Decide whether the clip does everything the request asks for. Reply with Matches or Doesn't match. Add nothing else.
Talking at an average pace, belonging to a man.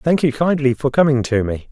Doesn't match